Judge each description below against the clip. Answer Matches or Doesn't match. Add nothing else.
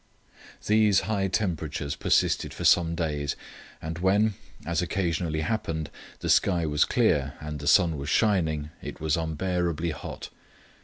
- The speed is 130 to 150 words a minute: Matches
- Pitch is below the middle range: Matches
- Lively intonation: Doesn't match